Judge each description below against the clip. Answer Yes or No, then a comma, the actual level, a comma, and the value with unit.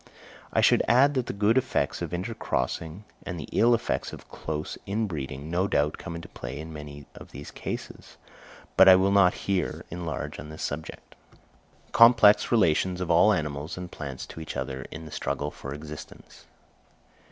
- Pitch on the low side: Yes, very low, 85 Hz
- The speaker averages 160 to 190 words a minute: Yes, average, 175 wpm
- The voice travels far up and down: No, average, 4.9 semitones